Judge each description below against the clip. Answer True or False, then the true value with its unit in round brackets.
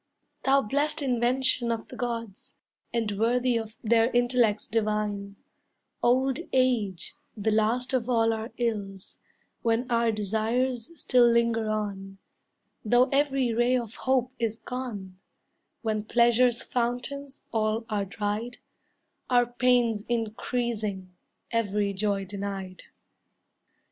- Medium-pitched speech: False (230 Hz)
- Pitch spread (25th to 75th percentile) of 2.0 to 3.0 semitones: True (2.7 semitones)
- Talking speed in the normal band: False (115 wpm)